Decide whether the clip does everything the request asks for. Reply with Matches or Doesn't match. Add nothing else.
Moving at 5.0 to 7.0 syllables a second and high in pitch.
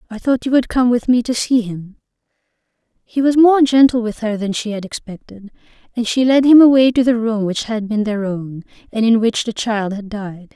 Matches